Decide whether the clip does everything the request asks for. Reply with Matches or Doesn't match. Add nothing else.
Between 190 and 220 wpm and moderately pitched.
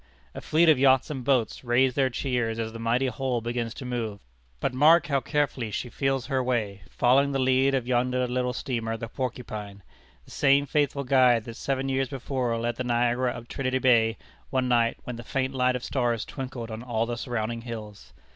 Doesn't match